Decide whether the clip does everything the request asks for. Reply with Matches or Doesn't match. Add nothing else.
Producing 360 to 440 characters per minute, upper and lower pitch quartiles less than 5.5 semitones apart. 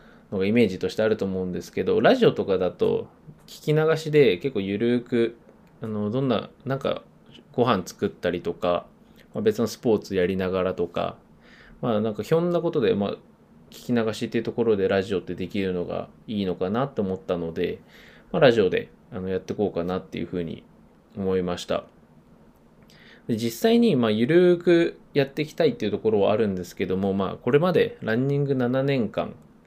Doesn't match